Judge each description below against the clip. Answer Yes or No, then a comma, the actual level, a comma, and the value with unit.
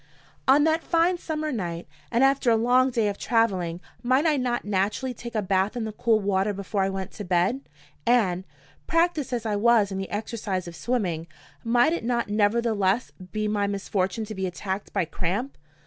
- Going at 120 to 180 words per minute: No, average, 190 wpm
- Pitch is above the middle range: Yes, high, 215 Hz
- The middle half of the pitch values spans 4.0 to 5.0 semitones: Yes, average, 4.3 semitones